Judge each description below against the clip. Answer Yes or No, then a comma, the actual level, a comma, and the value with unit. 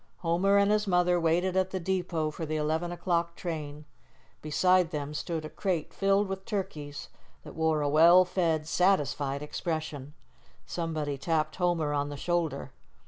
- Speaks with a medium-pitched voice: Yes, medium, 165 Hz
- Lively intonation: No, average, 3.2 semitones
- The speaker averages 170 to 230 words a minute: No, average, 155 wpm